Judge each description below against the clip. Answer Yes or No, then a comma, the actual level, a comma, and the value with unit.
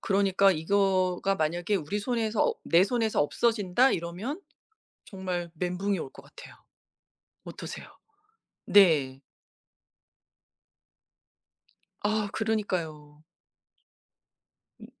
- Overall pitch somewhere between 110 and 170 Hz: No, high, 190 Hz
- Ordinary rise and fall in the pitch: Yes, average, 3.6 semitones